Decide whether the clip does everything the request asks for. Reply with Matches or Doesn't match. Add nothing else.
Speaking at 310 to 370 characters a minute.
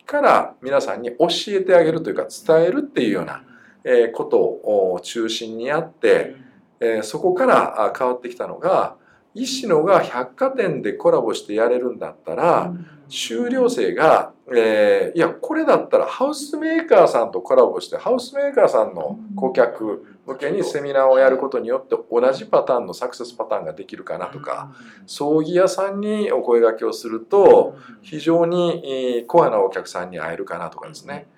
Matches